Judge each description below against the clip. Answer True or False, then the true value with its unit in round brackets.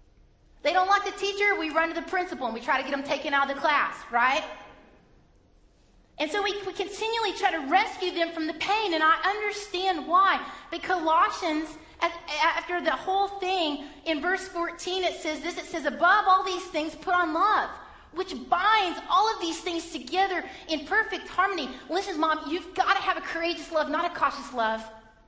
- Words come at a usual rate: True (195 wpm)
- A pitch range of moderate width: True (3.3 semitones)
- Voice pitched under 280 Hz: False (345 Hz)